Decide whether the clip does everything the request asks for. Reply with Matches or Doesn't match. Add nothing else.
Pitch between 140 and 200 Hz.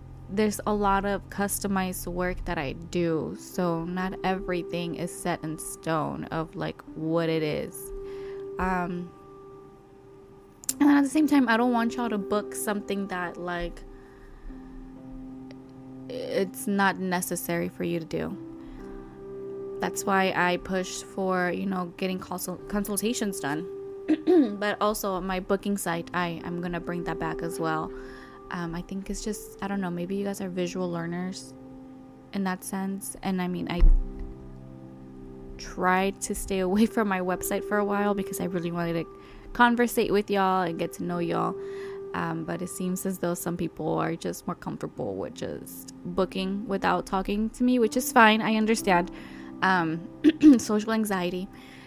Matches